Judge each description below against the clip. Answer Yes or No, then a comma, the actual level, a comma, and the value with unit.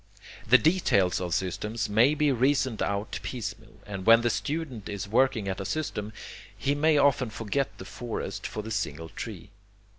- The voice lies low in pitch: Yes, low, 110 Hz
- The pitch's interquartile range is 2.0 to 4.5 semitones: No, average, 5.0 semitones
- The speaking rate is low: No, average, 170 wpm